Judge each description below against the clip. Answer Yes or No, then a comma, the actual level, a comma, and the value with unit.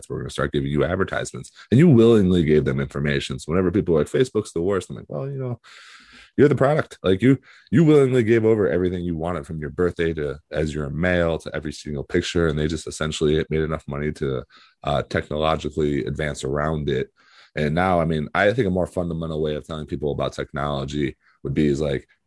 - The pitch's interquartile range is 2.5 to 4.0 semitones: Yes, average, 3.6 semitones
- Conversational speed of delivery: No, fast, 215 wpm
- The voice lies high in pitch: No, very low, 80 Hz